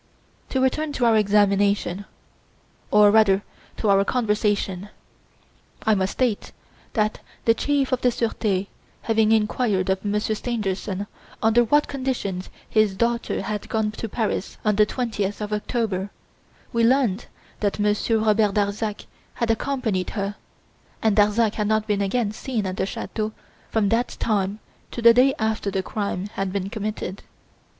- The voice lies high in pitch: Yes, high, 215 Hz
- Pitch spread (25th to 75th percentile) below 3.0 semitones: Yes, narrow, 2.4 semitones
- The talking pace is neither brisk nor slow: Yes, average, 150 wpm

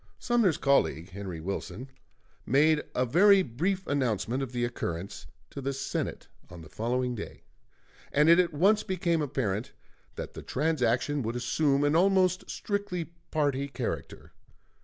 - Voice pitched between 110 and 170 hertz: Yes, medium, 140 Hz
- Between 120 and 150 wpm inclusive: Yes, average, 140 wpm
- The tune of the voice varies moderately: No, wide, 6.0 semitones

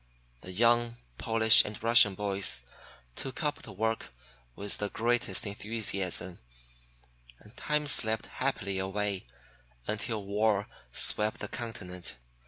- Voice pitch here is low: Yes, low, 105 Hz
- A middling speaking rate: No, slow, 115 wpm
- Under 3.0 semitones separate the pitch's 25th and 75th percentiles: Yes, narrow, 2.6 semitones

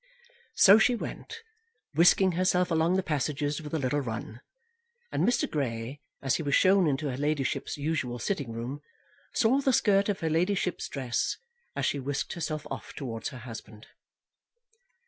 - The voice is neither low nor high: Yes, medium, 150 Hz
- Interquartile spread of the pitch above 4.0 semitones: Yes, wide, 5.6 semitones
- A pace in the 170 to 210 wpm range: No, average, 160 wpm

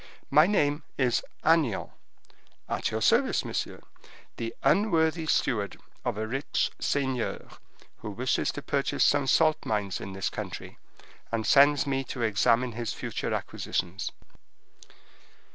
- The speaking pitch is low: Yes, low, 130 Hz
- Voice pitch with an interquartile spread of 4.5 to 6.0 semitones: Yes, average, 4.8 semitones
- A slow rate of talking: Yes, slow, 125 wpm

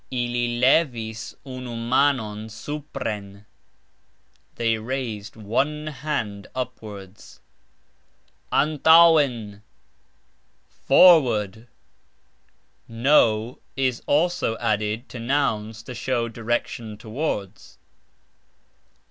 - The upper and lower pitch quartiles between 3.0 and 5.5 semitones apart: Yes, average, 4.0 semitones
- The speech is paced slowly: Yes, slow, 70 wpm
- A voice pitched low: Yes, low, 120 Hz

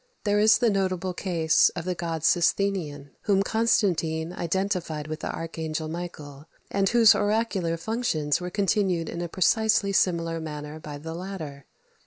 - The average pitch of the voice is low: No, medium, 175 Hz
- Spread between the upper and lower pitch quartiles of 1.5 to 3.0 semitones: No, average, 3.8 semitones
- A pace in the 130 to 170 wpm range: Yes, average, 150 wpm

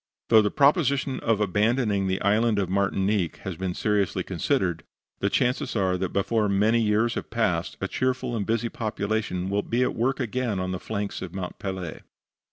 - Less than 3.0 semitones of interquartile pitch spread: No, average, 3.4 semitones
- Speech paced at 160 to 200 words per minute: Yes, average, 180 wpm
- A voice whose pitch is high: No, low, 105 Hz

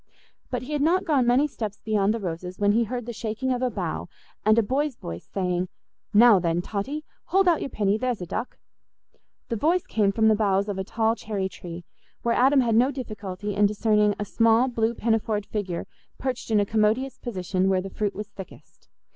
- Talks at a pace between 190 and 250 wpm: Yes, fast, 205 wpm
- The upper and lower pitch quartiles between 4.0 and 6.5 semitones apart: No, average, 3.6 semitones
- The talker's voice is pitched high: Yes, high, 220 Hz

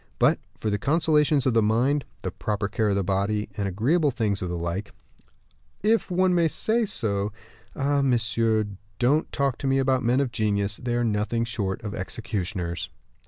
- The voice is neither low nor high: No, low, 115 Hz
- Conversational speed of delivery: Yes, average, 175 wpm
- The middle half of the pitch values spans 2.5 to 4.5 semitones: No, average, 5.2 semitones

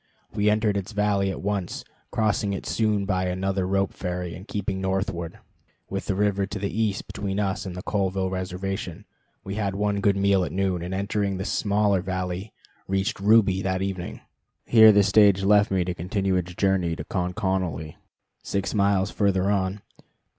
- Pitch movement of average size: No, narrow, 1.6 semitones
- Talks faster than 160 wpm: Yes, average, 170 wpm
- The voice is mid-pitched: No, very low, 95 Hz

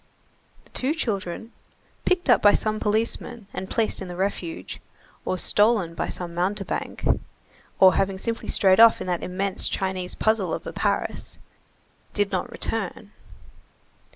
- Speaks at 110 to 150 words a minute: Yes, average, 145 wpm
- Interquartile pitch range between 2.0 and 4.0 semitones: Yes, average, 3.4 semitones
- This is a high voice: Yes, high, 200 Hz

